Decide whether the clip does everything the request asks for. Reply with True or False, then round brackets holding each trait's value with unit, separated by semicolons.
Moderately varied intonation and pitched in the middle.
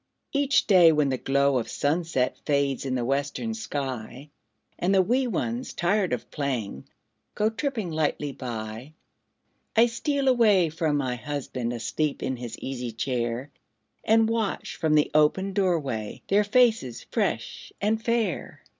False (8.5 semitones; 150 Hz)